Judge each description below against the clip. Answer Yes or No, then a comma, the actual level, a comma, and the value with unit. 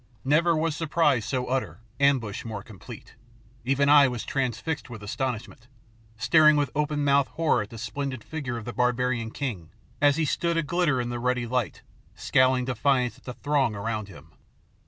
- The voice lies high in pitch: No, low, 130 Hz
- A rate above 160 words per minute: Yes, average, 170 wpm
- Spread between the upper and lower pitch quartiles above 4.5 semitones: No, average, 3.6 semitones